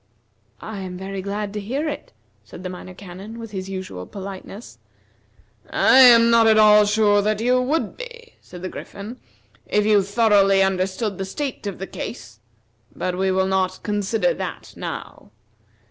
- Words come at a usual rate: Yes, average, 165 wpm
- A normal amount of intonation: Yes, average, 3.1 semitones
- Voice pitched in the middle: No, high, 205 Hz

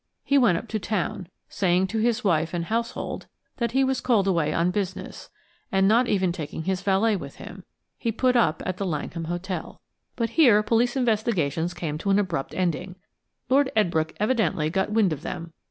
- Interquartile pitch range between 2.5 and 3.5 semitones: No, average, 4.9 semitones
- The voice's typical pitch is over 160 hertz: Yes, high, 190 Hz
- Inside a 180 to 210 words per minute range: Yes, average, 185 wpm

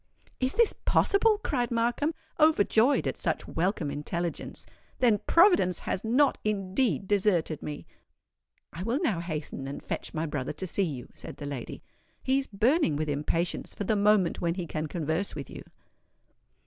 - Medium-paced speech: Yes, average, 160 wpm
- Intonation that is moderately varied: No, wide, 7.5 semitones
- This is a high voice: Yes, high, 195 Hz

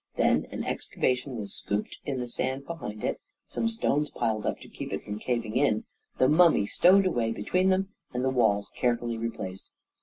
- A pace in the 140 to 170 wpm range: No, average, 185 wpm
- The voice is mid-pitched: No, low, 125 Hz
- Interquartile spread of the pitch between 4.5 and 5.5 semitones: Yes, average, 5.2 semitones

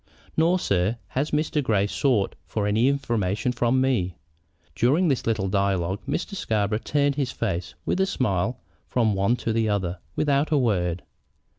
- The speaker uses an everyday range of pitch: No, wide, 5.9 semitones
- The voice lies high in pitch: No, low, 115 Hz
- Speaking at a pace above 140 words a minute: Yes, average, 160 wpm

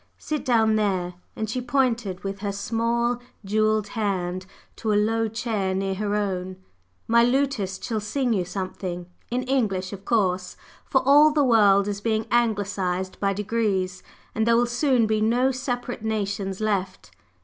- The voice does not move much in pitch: No, average, 3.4 semitones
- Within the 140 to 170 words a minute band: Yes, average, 160 wpm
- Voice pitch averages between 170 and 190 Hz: No, high, 215 Hz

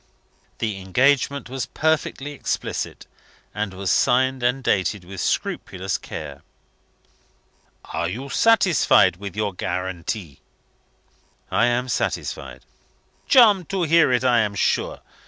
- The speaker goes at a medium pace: No, slow, 115 wpm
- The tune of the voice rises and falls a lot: Yes, wide, 6.4 semitones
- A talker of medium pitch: No, low, 120 Hz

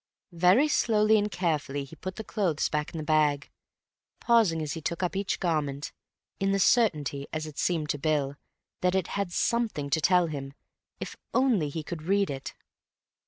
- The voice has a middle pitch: Yes, medium, 165 Hz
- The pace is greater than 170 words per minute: Yes, average, 180 wpm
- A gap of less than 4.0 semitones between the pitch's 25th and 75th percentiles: No, average, 4.7 semitones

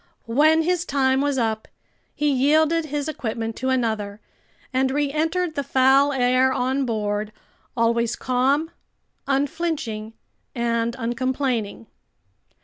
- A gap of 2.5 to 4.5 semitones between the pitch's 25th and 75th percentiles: Yes, average, 3.8 semitones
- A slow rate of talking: Yes, slow, 110 wpm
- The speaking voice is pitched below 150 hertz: No, very high, 260 Hz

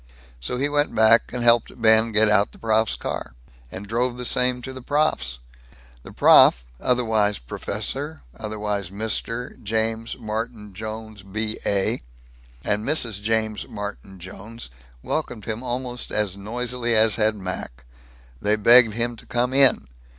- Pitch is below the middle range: Yes, low, 110 Hz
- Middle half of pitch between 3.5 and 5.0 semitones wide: No, narrow, 2.6 semitones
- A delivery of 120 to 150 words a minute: Yes, average, 145 wpm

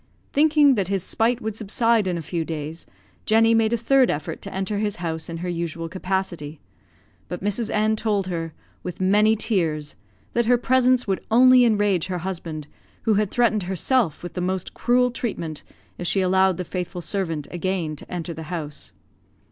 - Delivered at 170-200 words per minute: Yes, average, 180 wpm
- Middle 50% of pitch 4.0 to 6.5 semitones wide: Yes, average, 4.7 semitones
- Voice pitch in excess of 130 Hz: Yes, high, 190 Hz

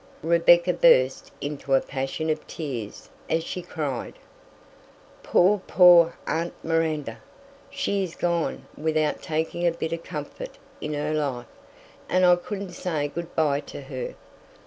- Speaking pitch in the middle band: Yes, medium, 160 Hz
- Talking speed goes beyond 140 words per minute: No, slow, 135 wpm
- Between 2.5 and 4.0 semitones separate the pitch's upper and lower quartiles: Yes, average, 3.2 semitones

